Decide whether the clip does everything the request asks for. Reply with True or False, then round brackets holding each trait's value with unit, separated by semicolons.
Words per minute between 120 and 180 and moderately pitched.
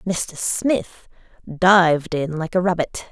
True (135 wpm; 175 Hz)